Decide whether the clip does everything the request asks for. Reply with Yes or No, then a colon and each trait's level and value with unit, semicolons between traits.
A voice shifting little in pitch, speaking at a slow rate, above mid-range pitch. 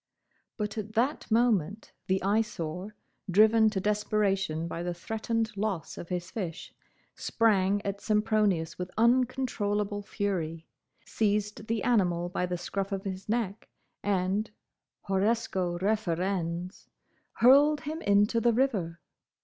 No: average, 3.3 semitones; slow, 115 wpm; high, 205 Hz